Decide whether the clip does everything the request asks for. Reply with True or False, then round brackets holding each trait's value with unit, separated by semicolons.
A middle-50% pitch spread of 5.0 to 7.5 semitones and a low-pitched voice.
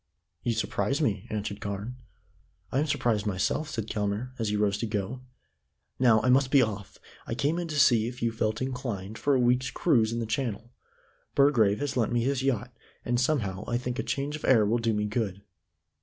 False (3.6 semitones; 115 Hz)